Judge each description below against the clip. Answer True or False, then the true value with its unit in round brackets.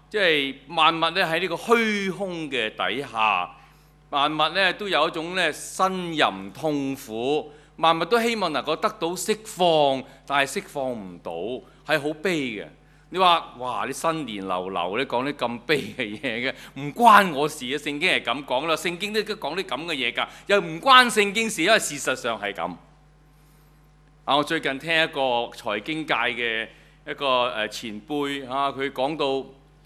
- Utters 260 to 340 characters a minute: False (230 characters per minute)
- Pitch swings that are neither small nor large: True (4.1 semitones)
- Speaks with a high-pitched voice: False (150 Hz)